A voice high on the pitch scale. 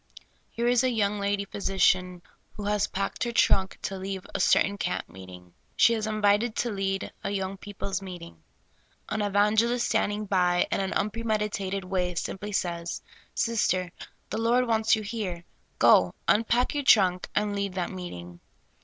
Yes: high, 200 Hz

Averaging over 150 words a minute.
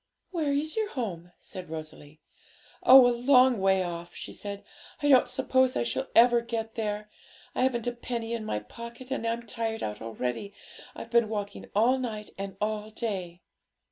Yes: average, 175 wpm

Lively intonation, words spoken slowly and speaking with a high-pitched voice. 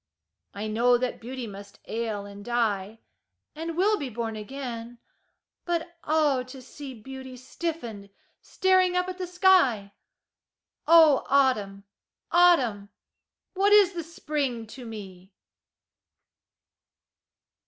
Yes: wide, 7.2 semitones; slow, 110 wpm; very high, 255 Hz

